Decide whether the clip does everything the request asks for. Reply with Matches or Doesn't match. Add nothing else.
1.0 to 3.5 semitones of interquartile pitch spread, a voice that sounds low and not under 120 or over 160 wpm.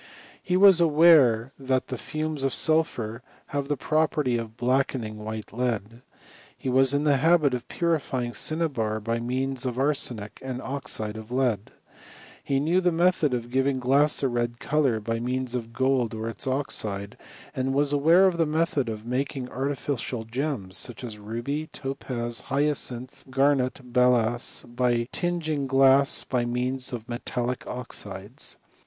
Matches